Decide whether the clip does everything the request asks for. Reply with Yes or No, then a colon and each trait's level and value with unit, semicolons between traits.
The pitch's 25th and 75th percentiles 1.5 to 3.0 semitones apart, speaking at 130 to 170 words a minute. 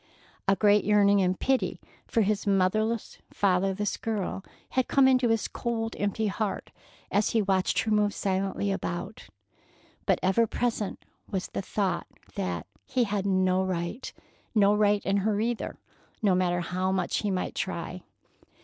Yes: narrow, 2.6 semitones; average, 150 wpm